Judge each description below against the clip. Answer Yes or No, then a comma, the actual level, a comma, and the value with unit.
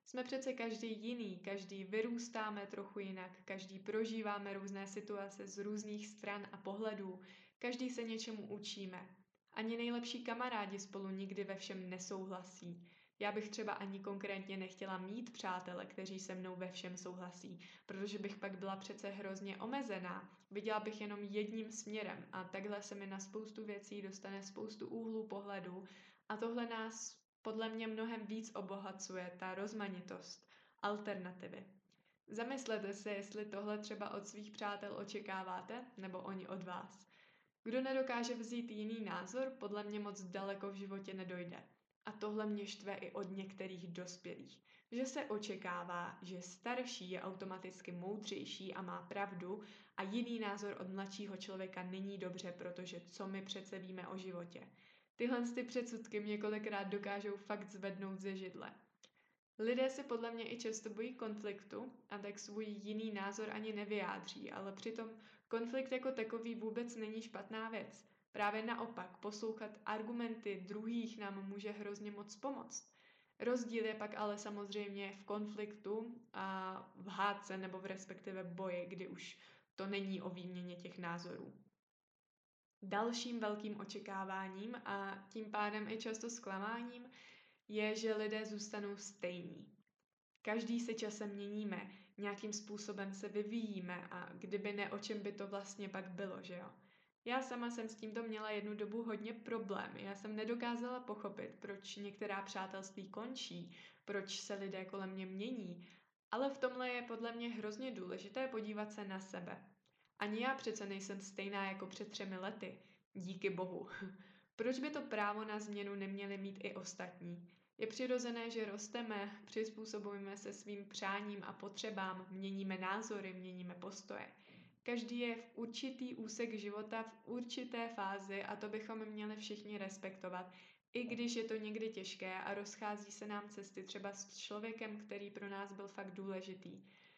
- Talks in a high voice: Yes, high, 205 Hz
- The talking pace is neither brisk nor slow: Yes, average, 150 wpm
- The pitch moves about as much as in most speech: No, narrow, 2.3 semitones